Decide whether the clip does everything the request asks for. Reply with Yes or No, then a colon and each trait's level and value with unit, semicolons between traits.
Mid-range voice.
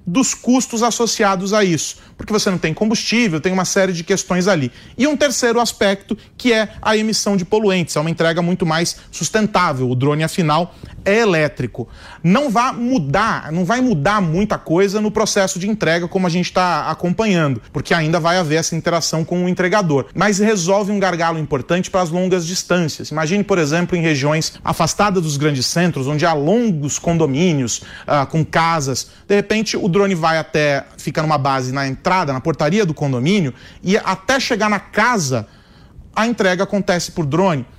Yes: medium, 180 Hz